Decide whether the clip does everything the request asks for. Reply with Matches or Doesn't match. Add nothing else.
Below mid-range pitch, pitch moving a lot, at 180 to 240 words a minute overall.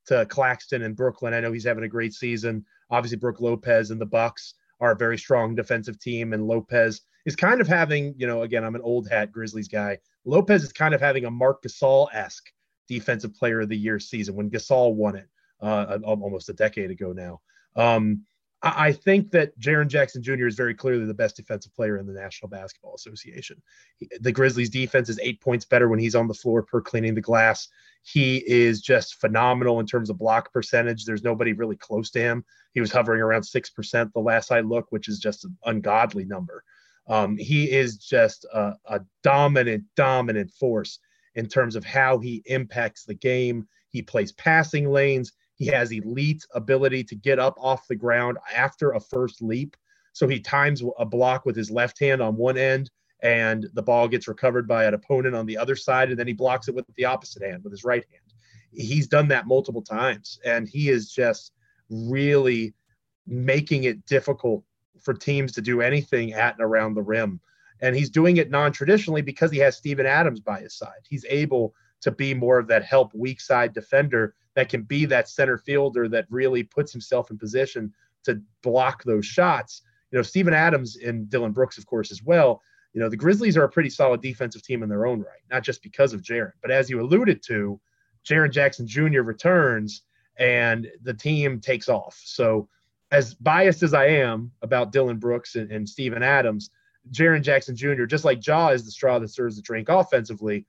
Doesn't match